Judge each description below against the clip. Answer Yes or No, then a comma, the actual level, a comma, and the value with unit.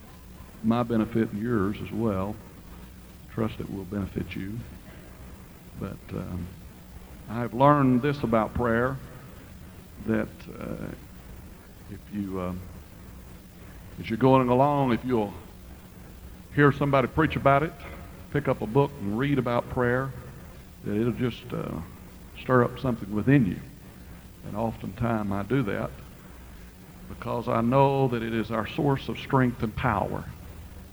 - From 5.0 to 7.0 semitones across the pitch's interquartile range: Yes, average, 5.3 semitones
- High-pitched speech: No, low, 110 Hz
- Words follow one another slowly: Yes, slow, 130 wpm